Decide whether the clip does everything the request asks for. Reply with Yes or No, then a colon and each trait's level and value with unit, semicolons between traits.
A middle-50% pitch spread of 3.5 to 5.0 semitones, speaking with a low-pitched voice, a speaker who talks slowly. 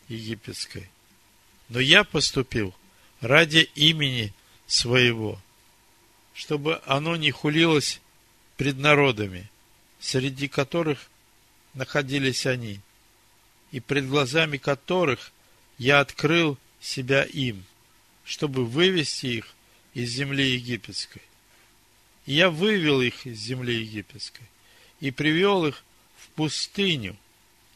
Yes: average, 4.6 semitones; low, 125 Hz; slow, 95 wpm